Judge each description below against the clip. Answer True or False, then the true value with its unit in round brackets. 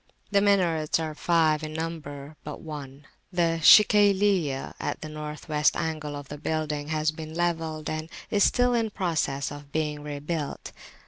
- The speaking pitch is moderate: True (155 Hz)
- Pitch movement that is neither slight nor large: False (2.2 semitones)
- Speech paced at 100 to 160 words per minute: True (155 wpm)